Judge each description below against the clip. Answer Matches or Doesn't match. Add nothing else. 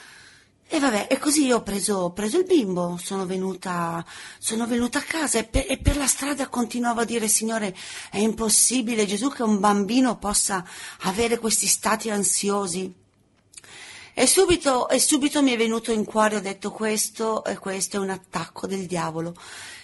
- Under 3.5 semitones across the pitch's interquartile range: Doesn't match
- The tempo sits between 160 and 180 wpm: Matches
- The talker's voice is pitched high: Matches